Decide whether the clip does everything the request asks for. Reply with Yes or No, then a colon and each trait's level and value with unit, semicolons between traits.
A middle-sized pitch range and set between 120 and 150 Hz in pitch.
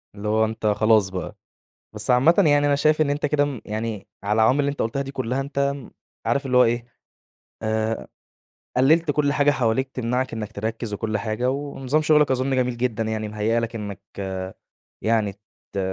Yes: average, 4.2 semitones; low, 125 Hz